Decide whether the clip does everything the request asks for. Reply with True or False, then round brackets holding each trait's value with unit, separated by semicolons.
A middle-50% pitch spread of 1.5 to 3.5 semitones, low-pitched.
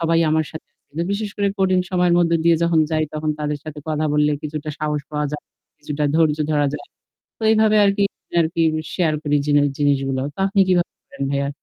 False (2.9 semitones; 155 Hz)